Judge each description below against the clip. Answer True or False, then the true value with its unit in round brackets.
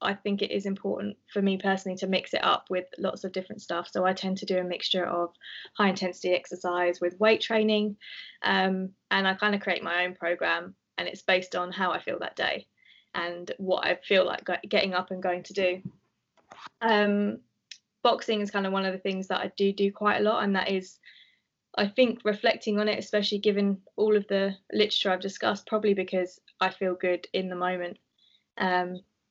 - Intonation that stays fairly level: True (2.1 semitones)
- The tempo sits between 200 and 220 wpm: True (205 wpm)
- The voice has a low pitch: False (190 Hz)